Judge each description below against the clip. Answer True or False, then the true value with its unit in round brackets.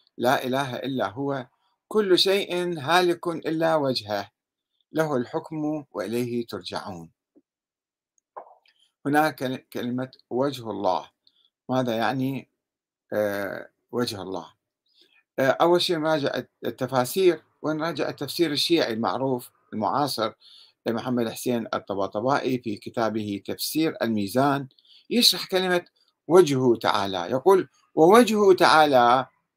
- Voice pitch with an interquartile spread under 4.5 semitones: False (5.2 semitones)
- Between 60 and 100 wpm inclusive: True (90 wpm)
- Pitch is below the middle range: True (130 Hz)